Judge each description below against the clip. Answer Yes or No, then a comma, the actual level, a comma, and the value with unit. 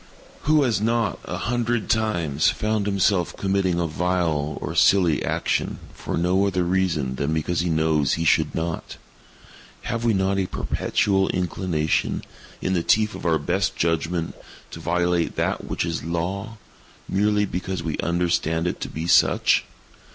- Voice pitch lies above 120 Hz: No, very low, 90 Hz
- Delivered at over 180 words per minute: No, average, 160 wpm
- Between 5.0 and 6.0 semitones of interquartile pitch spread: No, average, 3.2 semitones